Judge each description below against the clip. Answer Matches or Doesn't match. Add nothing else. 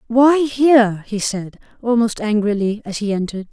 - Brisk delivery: Doesn't match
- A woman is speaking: Matches